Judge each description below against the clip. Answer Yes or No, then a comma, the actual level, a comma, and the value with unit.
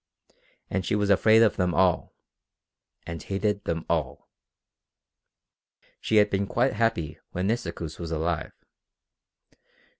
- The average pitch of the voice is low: Yes, very low, 95 Hz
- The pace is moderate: No, slow, 120 wpm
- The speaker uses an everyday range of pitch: Yes, average, 4.0 semitones